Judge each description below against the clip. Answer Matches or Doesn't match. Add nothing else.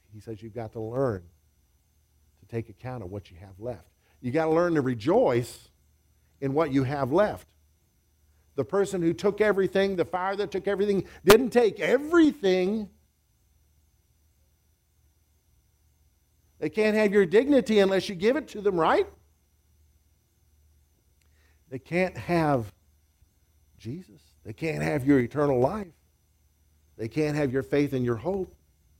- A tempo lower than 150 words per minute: Matches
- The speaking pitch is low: Matches